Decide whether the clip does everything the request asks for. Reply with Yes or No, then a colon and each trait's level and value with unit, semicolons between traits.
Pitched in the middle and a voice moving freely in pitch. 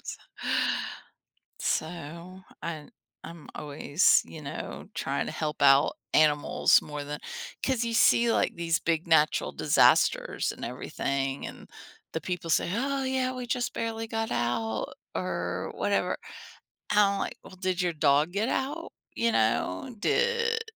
Yes: medium, 170 Hz; wide, 7.8 semitones